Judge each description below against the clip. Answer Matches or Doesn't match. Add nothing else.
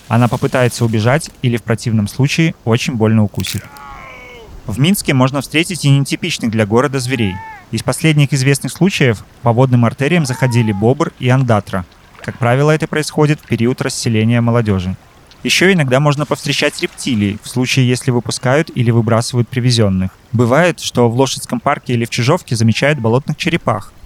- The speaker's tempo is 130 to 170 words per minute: Matches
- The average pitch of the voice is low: Matches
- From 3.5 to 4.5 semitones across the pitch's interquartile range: Matches